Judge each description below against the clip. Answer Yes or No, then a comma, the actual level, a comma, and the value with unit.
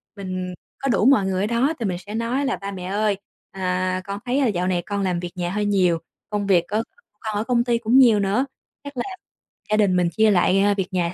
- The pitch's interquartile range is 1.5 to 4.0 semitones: Yes, average, 3.7 semitones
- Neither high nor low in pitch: No, high, 200 Hz